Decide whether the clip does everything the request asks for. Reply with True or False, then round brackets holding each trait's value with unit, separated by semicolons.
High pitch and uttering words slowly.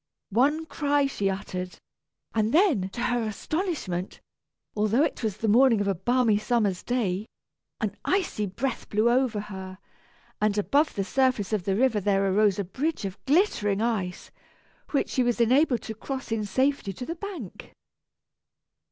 False (220 Hz; 160 wpm)